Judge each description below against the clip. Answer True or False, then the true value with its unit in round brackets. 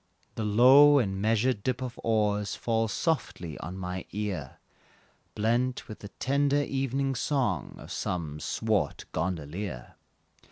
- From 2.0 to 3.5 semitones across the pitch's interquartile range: False (5.5 semitones)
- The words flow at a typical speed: False (125 wpm)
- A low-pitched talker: True (110 Hz)